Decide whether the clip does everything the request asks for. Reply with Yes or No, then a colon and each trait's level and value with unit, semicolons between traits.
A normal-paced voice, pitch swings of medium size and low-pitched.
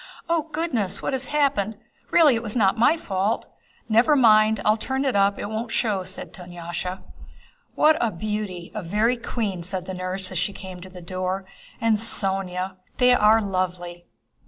No: average, 170 wpm; average, 3.9 semitones; high, 205 Hz